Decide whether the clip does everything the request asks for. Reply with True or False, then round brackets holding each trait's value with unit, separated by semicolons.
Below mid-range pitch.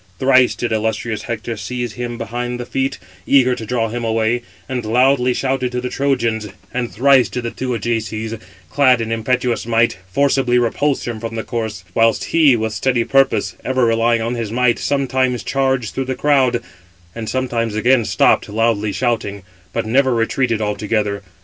True (120 Hz)